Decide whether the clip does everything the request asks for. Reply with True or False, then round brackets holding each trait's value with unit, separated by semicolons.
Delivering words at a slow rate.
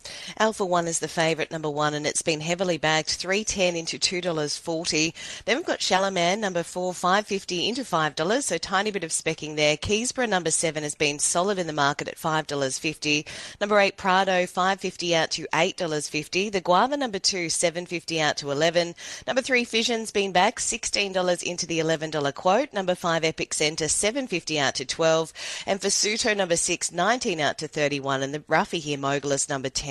False (185 wpm)